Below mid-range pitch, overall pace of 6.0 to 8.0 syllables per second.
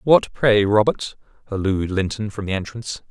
No: low, 105 Hz; 4.9 syllables/s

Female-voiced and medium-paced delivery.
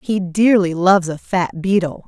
Yes: female; average, 175 wpm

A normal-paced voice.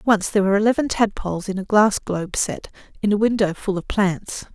No: fast, 210 wpm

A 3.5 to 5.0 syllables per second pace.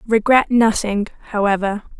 Yes: 4.7 syllables/s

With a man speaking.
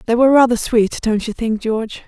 No: female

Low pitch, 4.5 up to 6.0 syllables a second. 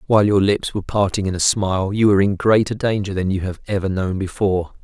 No: low, 100 Hz; 6.4 syllables/s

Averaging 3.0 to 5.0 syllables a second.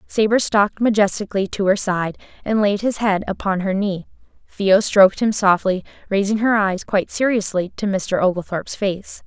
No: 5.2 syllables/s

